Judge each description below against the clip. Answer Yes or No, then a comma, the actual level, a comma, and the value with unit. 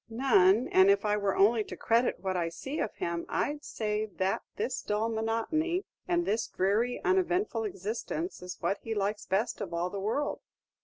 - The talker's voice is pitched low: No, high, 215 Hz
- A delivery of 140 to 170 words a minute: No, average, 190 wpm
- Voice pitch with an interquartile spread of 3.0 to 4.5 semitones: Yes, average, 4.1 semitones